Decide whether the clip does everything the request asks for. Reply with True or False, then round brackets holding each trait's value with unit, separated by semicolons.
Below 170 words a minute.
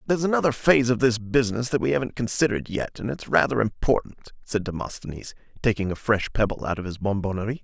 False (195 wpm)